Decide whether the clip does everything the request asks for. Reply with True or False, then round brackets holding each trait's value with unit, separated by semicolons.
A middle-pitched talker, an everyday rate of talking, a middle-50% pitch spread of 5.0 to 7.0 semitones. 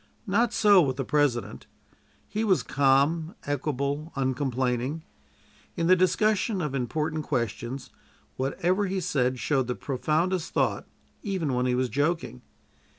False (145 Hz; 130 wpm; 5.6 semitones)